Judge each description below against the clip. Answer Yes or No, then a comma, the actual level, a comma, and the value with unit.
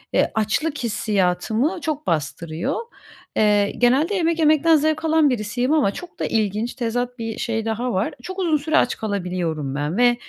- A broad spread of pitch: Yes, wide, 7.1 semitones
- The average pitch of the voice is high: Yes, high, 240 Hz